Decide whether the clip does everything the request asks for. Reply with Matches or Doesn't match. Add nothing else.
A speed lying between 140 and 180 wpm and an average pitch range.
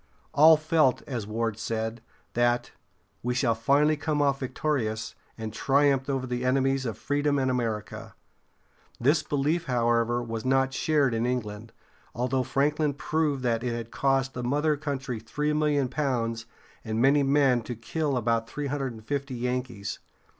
Matches